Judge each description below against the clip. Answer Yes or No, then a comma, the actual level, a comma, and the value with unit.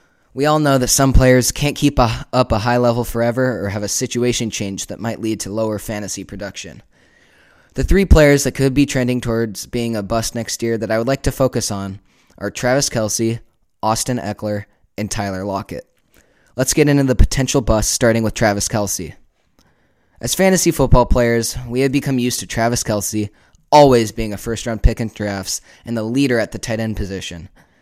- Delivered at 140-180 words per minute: No, average, 195 wpm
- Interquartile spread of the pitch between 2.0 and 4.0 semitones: Yes, average, 3.6 semitones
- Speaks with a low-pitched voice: Yes, low, 115 Hz